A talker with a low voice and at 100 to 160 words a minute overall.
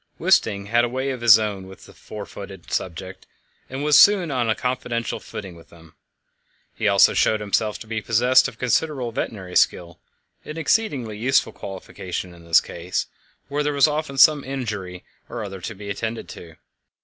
No: low, 110 Hz; average, 180 wpm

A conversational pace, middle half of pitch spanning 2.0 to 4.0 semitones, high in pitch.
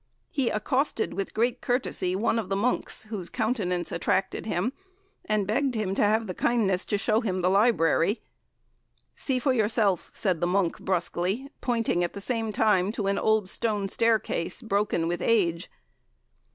Yes: average, 165 wpm; average, 3.7 semitones; high, 210 Hz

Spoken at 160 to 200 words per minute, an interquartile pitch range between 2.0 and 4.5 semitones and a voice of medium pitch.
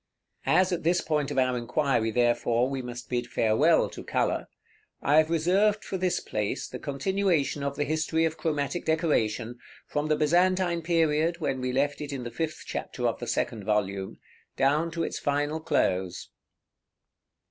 No: average, 170 wpm; average, 5.1 semitones; medium, 145 Hz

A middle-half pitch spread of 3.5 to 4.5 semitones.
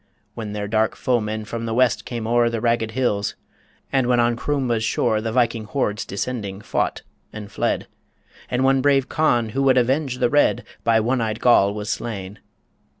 No: average, 2.8 semitones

